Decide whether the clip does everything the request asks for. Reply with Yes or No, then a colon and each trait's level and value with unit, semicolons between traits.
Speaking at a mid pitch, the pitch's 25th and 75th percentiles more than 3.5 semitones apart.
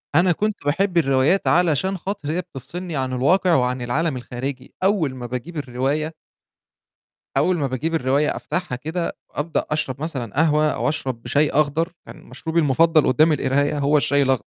Yes: medium, 150 Hz; average, 4.0 semitones